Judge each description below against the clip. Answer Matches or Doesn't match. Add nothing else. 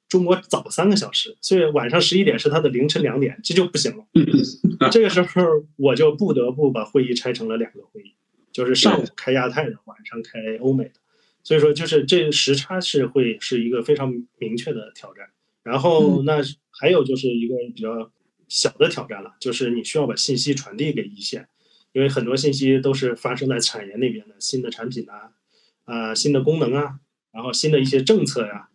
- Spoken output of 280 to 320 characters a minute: Matches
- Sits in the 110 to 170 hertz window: Matches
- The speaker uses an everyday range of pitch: Matches